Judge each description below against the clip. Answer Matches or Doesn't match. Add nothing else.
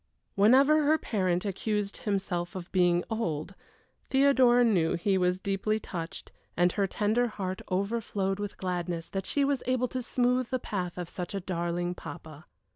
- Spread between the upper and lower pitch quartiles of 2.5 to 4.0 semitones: Doesn't match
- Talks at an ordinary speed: Matches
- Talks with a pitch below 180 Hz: Doesn't match